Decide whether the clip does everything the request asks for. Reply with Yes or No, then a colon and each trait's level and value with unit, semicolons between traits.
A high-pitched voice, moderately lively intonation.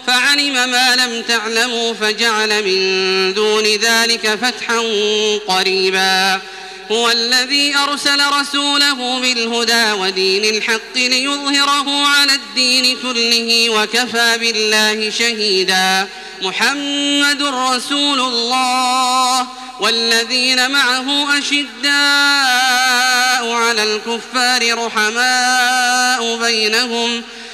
Yes: high, 235 Hz; average, 3.0 semitones